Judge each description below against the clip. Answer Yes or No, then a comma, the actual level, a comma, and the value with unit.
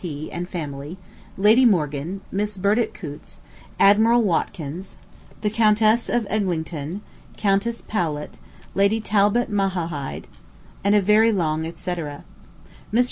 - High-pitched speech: Yes, high, 195 Hz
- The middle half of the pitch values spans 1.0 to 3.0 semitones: No, average, 4.8 semitones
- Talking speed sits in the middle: No, slow, 125 wpm